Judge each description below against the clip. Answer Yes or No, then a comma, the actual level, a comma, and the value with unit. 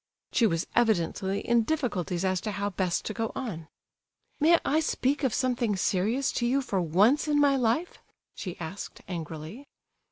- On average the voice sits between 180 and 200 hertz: No, high, 220 Hz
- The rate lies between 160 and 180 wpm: Yes, average, 165 wpm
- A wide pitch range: Yes, wide, 6.1 semitones